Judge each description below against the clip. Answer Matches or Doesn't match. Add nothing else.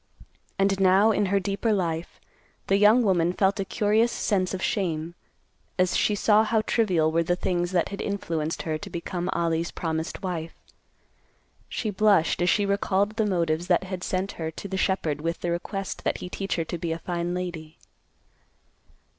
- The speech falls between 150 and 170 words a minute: Doesn't match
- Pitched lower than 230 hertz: Matches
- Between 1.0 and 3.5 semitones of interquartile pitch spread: Matches